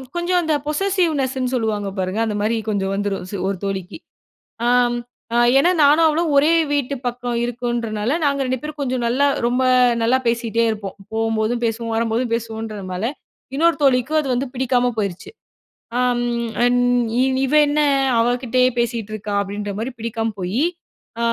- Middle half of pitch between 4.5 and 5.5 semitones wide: No, average, 3.5 semitones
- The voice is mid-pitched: No, high, 240 Hz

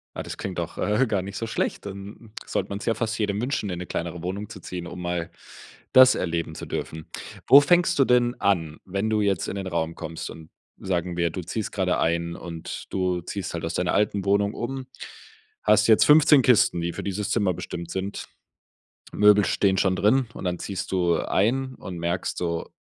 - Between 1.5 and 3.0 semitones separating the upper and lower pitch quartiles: No, average, 3.5 semitones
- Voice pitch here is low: Yes, very low, 95 Hz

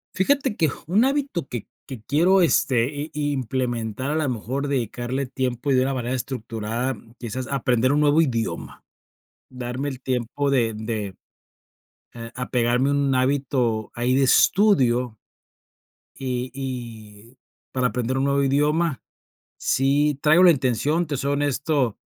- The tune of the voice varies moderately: Yes, average, 3.0 semitones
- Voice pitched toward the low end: Yes, low, 130 Hz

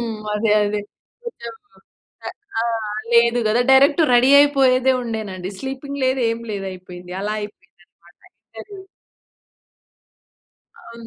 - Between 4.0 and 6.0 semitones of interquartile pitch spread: Yes, average, 4.4 semitones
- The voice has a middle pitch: No, high, 230 Hz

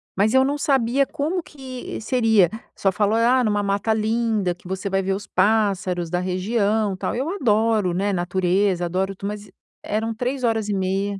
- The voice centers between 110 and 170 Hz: No, high, 210 Hz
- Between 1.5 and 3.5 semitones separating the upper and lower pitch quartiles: Yes, average, 3.2 semitones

